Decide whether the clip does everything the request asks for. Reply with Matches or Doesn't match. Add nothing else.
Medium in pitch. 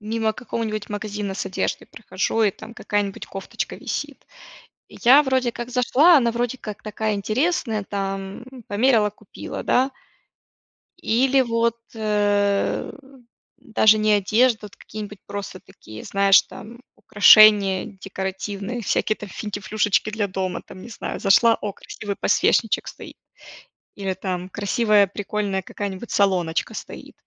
Doesn't match